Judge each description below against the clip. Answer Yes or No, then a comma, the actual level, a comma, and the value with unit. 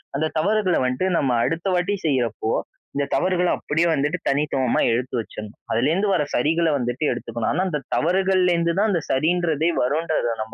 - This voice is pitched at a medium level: Yes, medium, 155 Hz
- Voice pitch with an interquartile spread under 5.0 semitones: No, wide, 5.5 semitones